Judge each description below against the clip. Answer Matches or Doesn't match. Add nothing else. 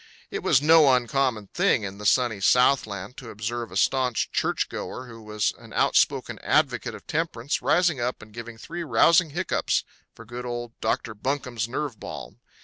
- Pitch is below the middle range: Matches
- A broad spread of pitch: Doesn't match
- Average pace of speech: Matches